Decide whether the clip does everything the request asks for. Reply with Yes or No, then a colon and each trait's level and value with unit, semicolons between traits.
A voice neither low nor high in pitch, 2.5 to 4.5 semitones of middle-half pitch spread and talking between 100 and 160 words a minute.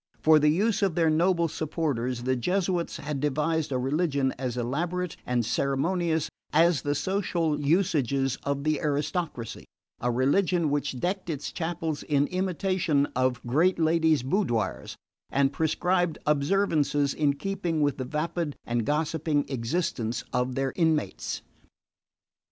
Yes: medium, 150 Hz; average, 3.9 semitones; slow, 135 wpm